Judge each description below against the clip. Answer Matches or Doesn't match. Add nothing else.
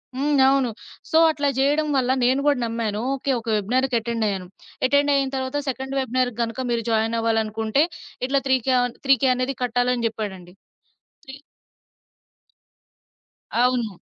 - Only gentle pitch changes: Doesn't match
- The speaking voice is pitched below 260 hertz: Matches